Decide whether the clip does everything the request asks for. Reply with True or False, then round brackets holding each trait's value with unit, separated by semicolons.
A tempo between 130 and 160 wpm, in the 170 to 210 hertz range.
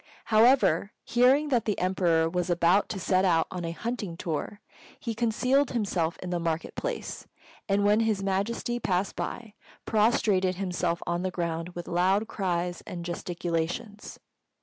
True (150 wpm; 190 Hz)